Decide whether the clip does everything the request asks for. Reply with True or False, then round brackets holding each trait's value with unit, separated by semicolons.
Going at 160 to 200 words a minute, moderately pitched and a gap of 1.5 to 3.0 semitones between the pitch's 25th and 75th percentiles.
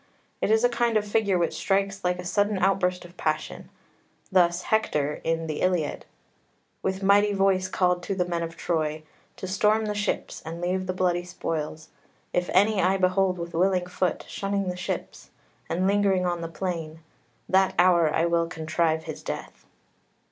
True (175 wpm; 180 Hz; 2.4 semitones)